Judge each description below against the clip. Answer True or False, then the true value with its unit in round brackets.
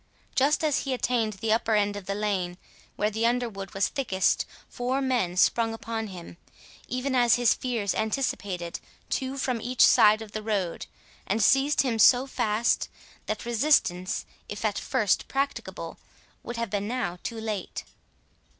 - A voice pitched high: True (225 Hz)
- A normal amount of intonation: True (3.6 semitones)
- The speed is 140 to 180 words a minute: True (160 wpm)